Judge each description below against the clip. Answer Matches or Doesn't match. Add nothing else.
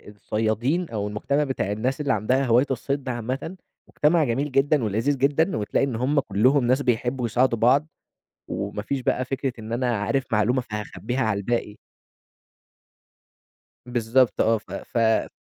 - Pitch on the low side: Matches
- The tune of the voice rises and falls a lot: Doesn't match